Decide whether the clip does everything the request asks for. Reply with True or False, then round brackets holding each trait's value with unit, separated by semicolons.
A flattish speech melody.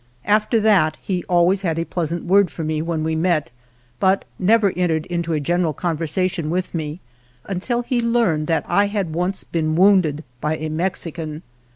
False (3.4 semitones)